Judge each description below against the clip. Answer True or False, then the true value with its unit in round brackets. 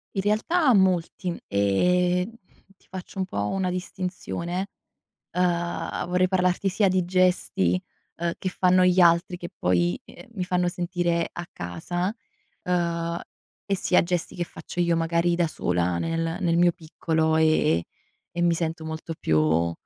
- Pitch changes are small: True (1.8 semitones)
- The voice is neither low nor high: True (175 Hz)